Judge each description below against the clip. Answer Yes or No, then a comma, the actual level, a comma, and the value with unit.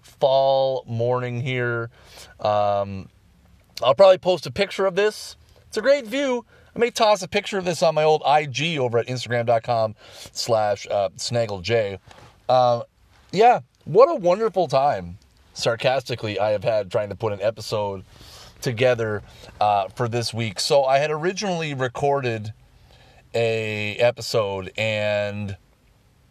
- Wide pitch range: Yes, wide, 6.3 semitones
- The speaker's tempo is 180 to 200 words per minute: No, slow, 135 wpm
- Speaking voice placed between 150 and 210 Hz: No, low, 120 Hz